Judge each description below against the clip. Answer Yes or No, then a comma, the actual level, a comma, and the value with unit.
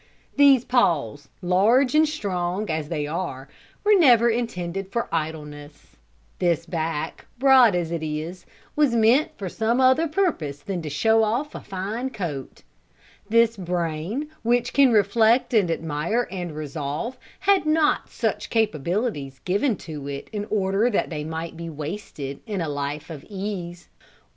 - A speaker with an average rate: Yes, average, 150 wpm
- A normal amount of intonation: No, wide, 6.9 semitones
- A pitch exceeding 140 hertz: Yes, high, 190 Hz